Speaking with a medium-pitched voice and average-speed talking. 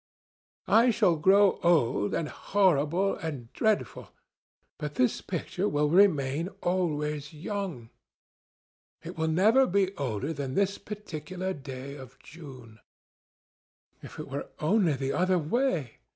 No: medium, 160 Hz; slow, 125 wpm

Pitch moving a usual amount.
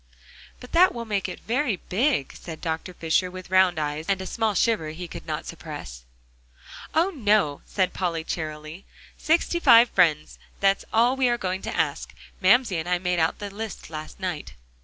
No: wide, 5.9 semitones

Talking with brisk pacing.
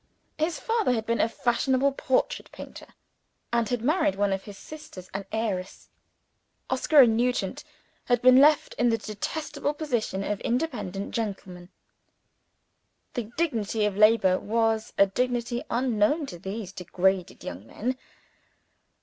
No: slow, 135 wpm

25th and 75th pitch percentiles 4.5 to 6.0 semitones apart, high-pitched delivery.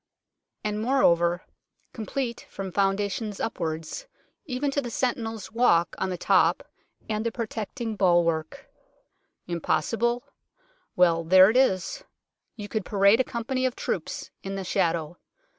Yes: average, 4.9 semitones; high, 210 Hz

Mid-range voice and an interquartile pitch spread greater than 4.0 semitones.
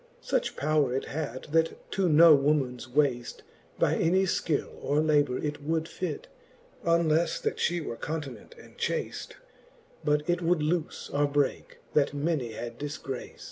No: medium, 150 Hz; average, 2.7 semitones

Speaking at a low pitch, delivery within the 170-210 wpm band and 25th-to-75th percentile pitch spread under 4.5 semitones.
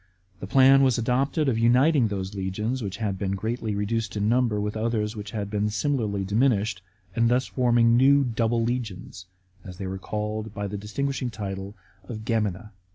Yes: low, 110 Hz; average, 180 wpm; average, 3.1 semitones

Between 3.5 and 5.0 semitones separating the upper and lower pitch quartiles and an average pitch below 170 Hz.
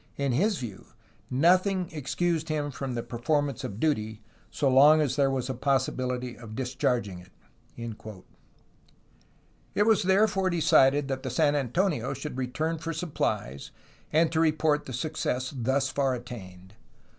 Yes: average, 4.2 semitones; low, 135 Hz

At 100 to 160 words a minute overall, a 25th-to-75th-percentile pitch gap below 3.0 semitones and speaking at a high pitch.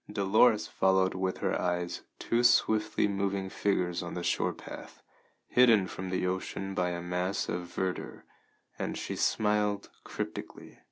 No: average, 145 wpm; narrow, 2.5 semitones; very low, 95 Hz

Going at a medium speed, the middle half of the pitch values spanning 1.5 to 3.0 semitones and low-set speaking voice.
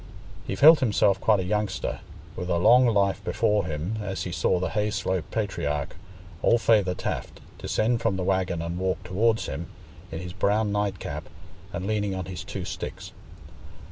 Yes: average, 170 wpm; average, 2.7 semitones; very low, 95 Hz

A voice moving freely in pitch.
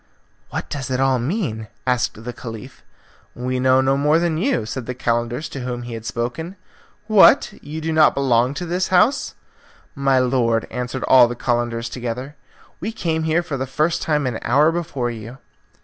No: average, 4.6 semitones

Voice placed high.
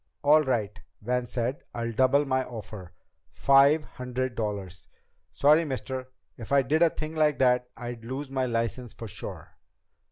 No: low, 125 Hz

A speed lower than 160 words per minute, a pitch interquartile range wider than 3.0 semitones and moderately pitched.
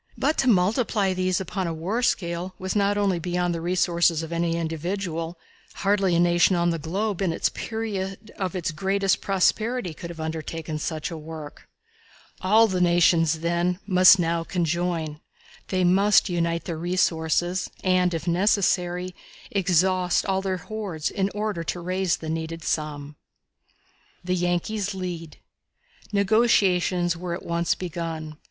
No: average, 145 wpm; narrow, 2.4 semitones; medium, 180 Hz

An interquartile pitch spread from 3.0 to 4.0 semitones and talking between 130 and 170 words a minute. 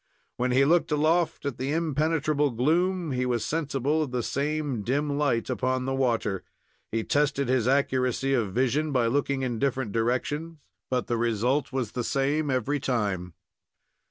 Yes: average, 3.3 semitones; average, 160 wpm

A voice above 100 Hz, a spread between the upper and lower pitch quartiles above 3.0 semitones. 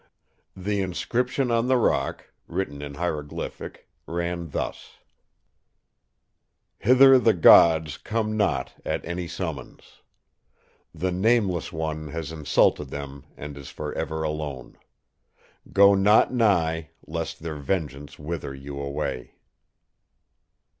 No: very low, 80 Hz; average, 5.2 semitones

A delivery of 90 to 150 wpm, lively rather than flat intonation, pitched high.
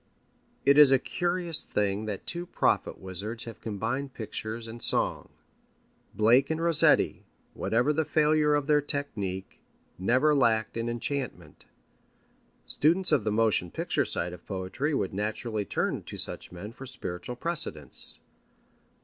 No: average, 140 wpm; wide, 6.0 semitones; low, 120 Hz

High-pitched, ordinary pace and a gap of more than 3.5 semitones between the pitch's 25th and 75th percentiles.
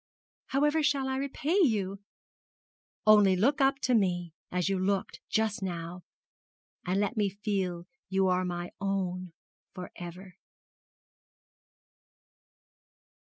No: high, 195 Hz; slow, 110 wpm; average, 4.0 semitones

